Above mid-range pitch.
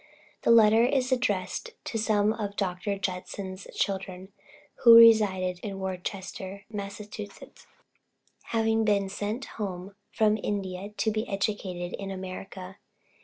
Yes: high, 200 Hz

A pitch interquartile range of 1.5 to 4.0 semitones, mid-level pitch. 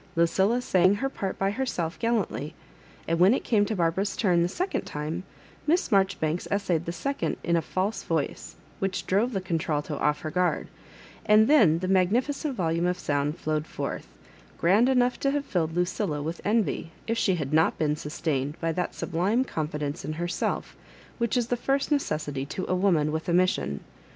No: average, 5.3 semitones; medium, 180 Hz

